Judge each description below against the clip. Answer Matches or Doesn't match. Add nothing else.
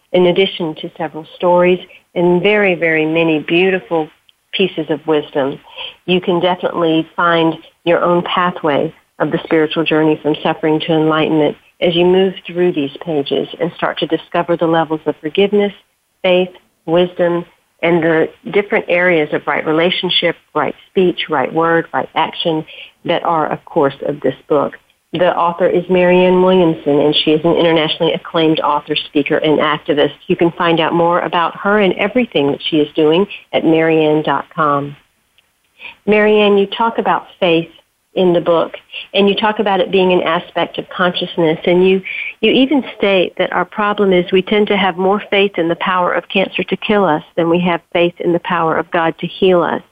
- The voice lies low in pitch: Doesn't match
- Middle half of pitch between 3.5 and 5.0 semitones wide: Doesn't match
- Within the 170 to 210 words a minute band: Matches